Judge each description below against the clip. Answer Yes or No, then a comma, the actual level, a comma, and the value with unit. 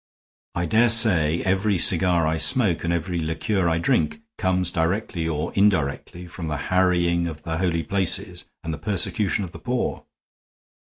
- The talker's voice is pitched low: Yes, very low, 85 Hz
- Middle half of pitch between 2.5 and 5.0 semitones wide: Yes, average, 3.1 semitones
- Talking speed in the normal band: Yes, average, 160 wpm